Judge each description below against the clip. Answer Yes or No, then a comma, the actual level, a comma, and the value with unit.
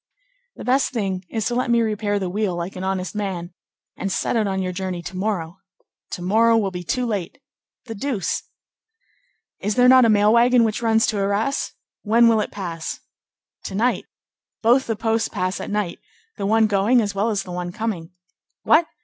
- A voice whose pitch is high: Yes, high, 210 Hz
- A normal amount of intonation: Yes, average, 3.4 semitones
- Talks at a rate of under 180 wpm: No, average, 195 wpm